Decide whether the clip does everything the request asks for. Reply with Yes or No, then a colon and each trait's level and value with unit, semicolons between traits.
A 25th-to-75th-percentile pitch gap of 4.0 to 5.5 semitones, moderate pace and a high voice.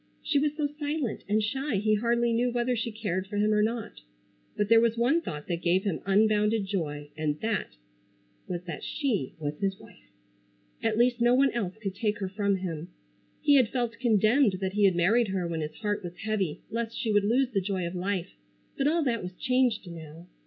No: average, 4.3 semitones; fast, 210 wpm; high, 210 Hz